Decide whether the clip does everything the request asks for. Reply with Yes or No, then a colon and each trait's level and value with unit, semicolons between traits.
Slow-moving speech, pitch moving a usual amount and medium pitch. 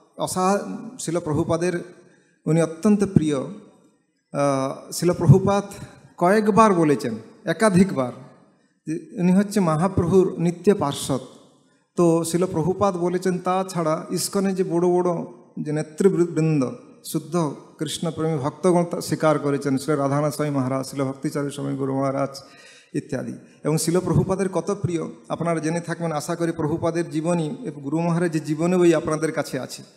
Yes: slow, 115 wpm; average, 3.1 semitones; medium, 165 Hz